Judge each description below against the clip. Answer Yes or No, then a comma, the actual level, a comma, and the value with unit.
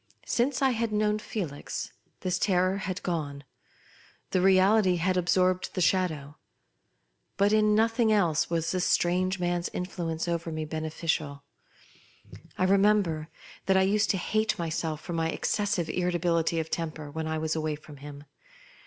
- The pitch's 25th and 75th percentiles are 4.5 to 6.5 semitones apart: No, average, 3.5 semitones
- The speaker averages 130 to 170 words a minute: Yes, average, 160 wpm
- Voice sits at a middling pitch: Yes, medium, 175 Hz